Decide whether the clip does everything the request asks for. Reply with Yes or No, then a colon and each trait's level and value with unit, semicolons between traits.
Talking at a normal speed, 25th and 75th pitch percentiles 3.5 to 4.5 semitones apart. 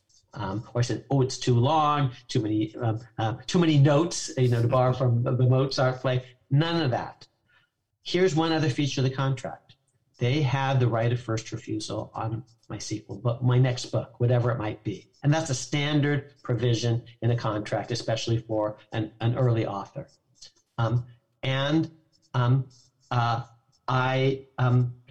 No: average, 170 wpm; narrow, 2.6 semitones